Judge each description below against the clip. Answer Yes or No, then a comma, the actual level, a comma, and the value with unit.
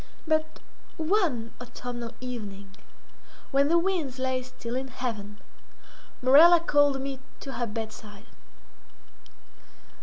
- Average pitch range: Yes, average, 4.5 semitones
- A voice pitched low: No, very high, 255 Hz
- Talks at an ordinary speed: No, slow, 100 wpm